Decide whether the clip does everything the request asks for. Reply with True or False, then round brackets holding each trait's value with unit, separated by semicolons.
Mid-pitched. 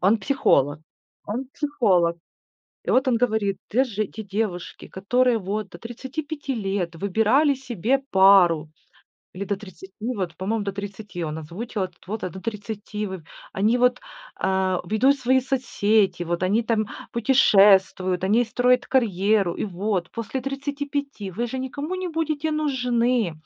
False (215 Hz)